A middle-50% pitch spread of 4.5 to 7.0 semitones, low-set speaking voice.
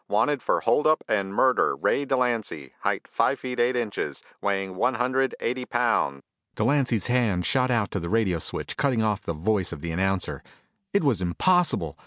Yes: average, 5.1 semitones; low, 115 Hz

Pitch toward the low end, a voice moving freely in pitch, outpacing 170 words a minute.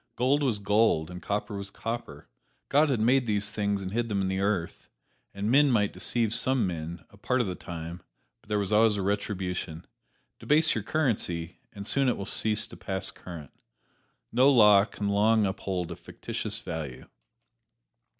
No: low, 105 Hz; average, 3.6 semitones; average, 180 wpm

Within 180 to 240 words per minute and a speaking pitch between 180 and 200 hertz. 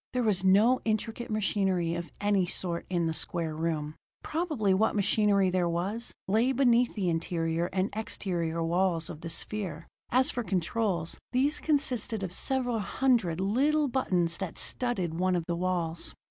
No: average, 160 wpm; high, 190 Hz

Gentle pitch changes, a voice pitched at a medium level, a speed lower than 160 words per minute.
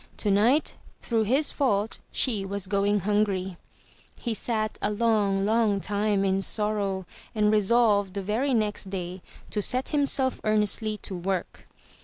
No: narrow, 2.3 semitones; high, 210 Hz; average, 140 wpm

